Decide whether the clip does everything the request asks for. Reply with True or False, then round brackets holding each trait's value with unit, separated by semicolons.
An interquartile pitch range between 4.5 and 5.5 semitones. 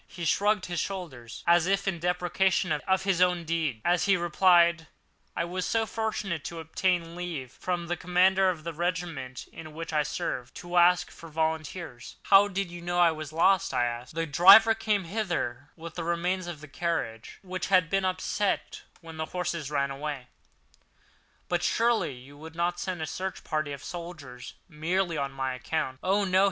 False (2.9 semitones)